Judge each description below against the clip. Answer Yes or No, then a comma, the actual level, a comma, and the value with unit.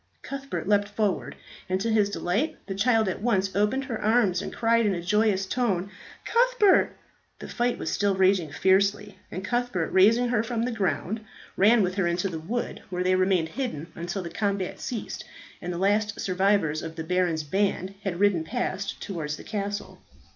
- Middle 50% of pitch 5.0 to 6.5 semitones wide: No, average, 3.5 semitones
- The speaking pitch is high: Yes, high, 200 Hz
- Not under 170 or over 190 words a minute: Yes, average, 185 wpm